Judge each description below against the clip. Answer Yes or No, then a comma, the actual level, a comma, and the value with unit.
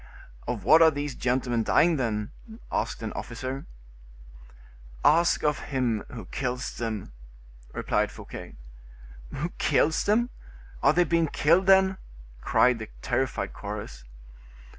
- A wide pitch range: Yes, wide, 5.7 semitones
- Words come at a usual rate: No, slow, 120 wpm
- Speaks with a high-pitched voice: No, low, 135 Hz